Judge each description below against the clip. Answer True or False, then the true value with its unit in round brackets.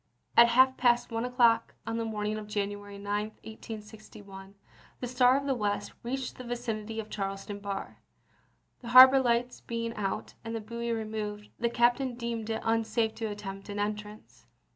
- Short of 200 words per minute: True (180 wpm)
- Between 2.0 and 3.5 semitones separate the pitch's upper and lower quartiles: True (2.4 semitones)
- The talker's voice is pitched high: True (225 Hz)